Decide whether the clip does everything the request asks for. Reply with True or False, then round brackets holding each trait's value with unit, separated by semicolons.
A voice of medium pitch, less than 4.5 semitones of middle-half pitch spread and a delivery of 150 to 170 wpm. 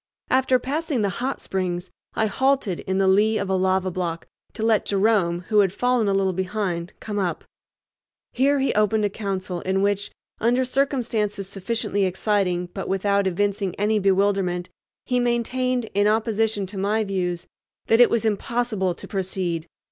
False (205 Hz; 3.1 semitones; 165 wpm)